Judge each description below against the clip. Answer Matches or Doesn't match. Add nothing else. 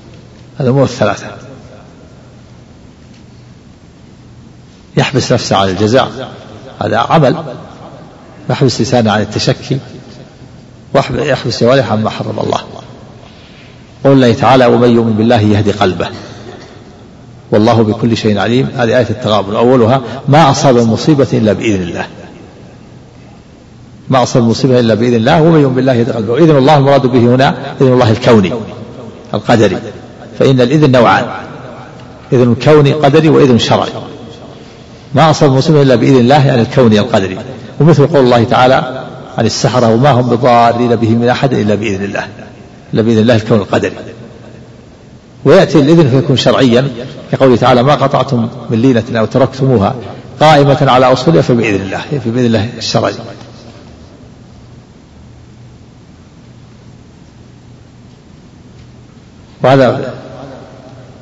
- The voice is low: Matches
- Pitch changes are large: Doesn't match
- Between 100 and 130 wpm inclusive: Matches